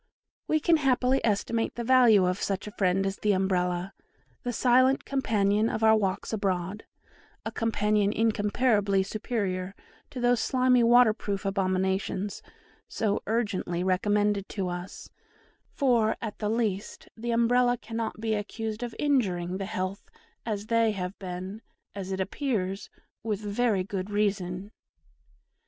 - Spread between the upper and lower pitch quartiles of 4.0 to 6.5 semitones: No, average, 3.2 semitones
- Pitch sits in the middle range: No, high, 210 Hz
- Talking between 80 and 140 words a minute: Yes, slow, 135 wpm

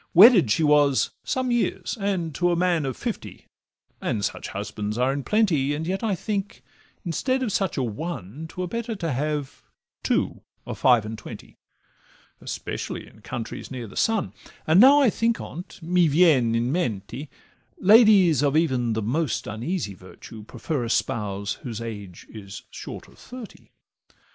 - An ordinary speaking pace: Yes, average, 165 wpm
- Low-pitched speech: No, medium, 150 Hz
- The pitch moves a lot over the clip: Yes, wide, 8.3 semitones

